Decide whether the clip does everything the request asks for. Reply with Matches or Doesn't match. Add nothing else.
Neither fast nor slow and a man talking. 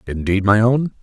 Matches